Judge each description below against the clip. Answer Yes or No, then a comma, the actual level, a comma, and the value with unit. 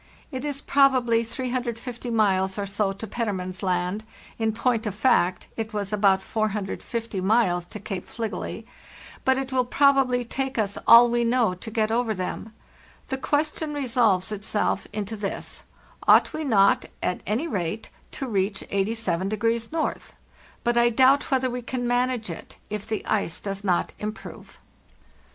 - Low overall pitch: No, high, 225 Hz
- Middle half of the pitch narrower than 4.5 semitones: Yes, average, 3.8 semitones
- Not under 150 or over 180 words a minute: Yes, average, 155 wpm